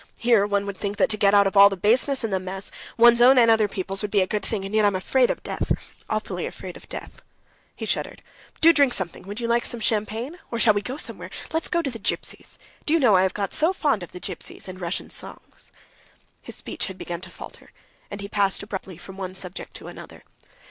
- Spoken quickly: Yes, fast, 245 wpm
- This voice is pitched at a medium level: No, high, 205 Hz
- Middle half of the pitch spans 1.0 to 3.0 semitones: No, average, 3.6 semitones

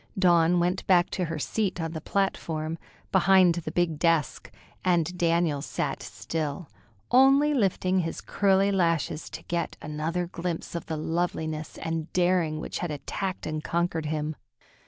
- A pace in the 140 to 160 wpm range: Yes, average, 150 wpm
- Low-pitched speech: No, medium, 170 Hz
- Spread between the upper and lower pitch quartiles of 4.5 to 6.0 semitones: No, narrow, 2.5 semitones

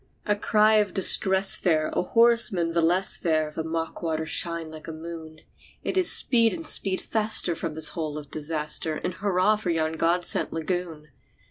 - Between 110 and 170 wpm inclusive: No, average, 185 wpm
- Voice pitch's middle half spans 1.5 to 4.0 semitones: Yes, average, 3.7 semitones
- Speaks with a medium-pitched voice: Yes, medium, 170 Hz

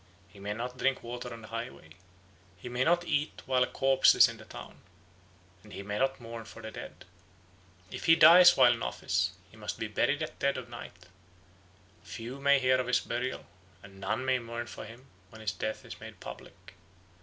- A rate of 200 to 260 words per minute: Yes, fast, 205 wpm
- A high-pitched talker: No, low, 120 Hz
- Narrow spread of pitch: No, average, 3.6 semitones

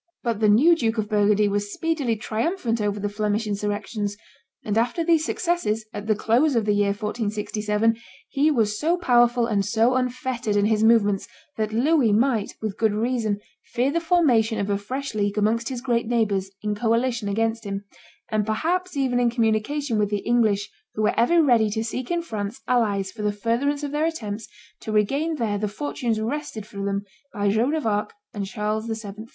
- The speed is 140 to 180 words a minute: No, average, 190 wpm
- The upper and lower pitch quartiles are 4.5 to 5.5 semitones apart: No, average, 3.4 semitones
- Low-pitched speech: No, high, 225 Hz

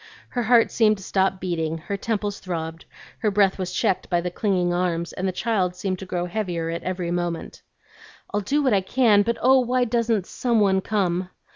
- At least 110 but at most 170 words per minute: No, average, 195 wpm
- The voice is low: No, high, 190 Hz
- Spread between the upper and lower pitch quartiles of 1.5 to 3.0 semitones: No, average, 3.6 semitones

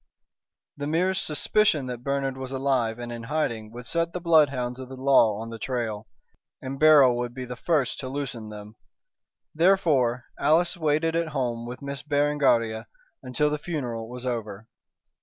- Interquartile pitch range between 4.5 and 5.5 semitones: No, average, 4.0 semitones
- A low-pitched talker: Yes, low, 130 Hz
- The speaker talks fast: No, average, 165 wpm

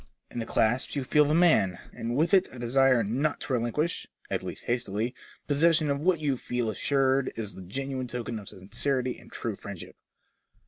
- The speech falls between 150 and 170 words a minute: No, average, 185 wpm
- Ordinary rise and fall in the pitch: Yes, average, 3.9 semitones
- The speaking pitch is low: Yes, low, 130 Hz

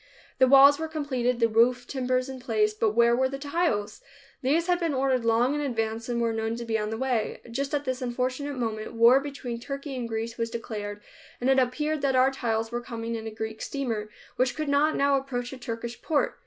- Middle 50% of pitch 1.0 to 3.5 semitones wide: Yes, average, 3.2 semitones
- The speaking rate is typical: No, fast, 220 wpm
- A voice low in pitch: No, very high, 250 Hz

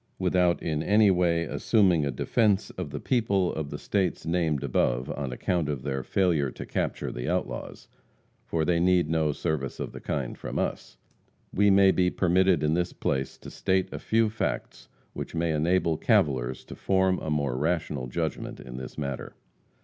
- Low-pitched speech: Yes, very low, 80 Hz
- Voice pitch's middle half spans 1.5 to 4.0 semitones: No, average, 4.6 semitones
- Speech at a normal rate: Yes, average, 180 wpm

